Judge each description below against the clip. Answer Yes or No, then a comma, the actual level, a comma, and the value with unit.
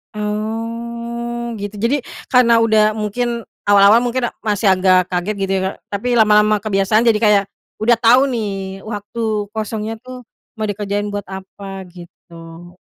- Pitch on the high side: Yes, high, 215 Hz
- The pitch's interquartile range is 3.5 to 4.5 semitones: No, average, 2.8 semitones